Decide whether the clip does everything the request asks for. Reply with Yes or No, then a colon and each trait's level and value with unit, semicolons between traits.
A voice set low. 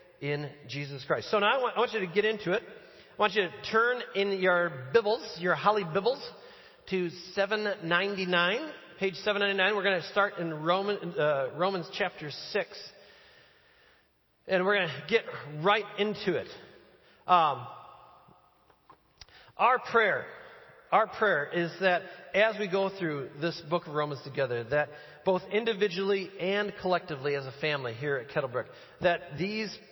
No: high, 190 Hz